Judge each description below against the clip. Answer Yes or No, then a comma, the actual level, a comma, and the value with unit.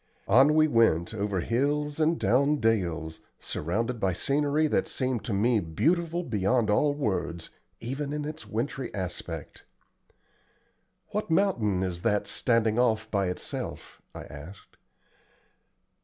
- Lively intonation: Yes, wide, 7.2 semitones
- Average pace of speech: No, slow, 125 wpm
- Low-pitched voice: Yes, low, 115 Hz